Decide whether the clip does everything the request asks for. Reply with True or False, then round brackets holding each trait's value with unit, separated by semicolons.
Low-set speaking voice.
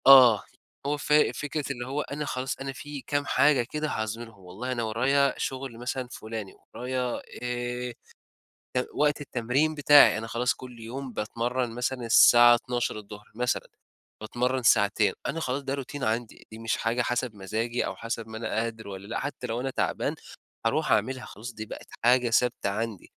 True (125 Hz)